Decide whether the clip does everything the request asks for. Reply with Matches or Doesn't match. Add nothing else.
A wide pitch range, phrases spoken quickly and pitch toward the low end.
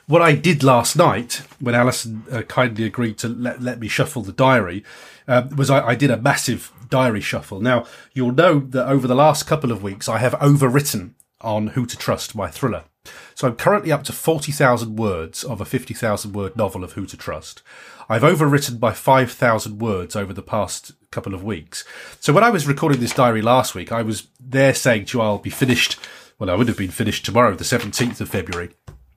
Doesn't match